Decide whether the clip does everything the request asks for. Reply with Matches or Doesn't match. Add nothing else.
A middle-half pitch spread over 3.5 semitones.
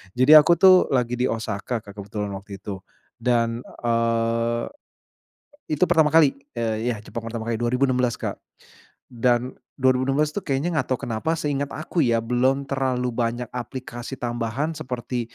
Doesn't match